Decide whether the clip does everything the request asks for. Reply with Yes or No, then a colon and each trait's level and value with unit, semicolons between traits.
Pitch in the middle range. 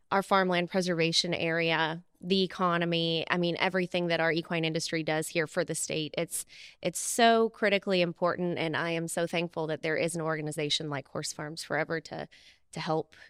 Yes: medium, 170 Hz